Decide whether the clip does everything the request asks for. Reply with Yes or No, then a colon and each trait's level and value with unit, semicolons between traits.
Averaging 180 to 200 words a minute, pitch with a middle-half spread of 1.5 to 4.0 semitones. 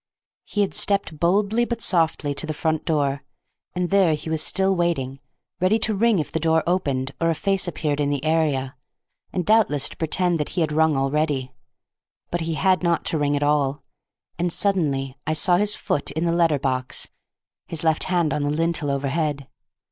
Yes: average, 195 wpm; average, 3.6 semitones